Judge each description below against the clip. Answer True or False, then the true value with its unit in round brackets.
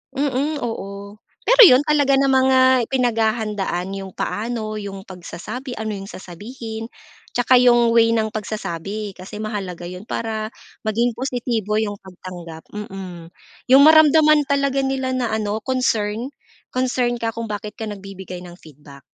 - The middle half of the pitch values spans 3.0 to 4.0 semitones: False (4.4 semitones)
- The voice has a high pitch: True (220 Hz)